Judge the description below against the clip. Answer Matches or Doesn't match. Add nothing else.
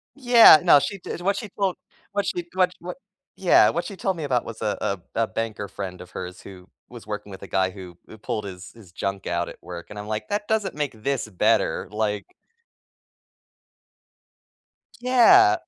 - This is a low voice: Matches